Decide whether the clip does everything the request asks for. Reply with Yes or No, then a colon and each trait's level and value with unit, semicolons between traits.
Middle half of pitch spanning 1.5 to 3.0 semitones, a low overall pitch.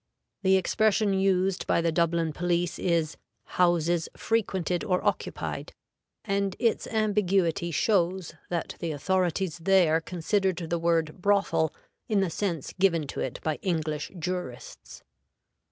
No: average, 2.7 semitones; medium, 175 Hz